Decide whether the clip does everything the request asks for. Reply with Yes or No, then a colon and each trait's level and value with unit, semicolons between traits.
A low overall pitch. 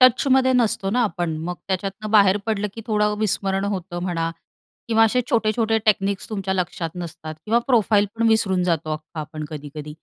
No: high, 195 Hz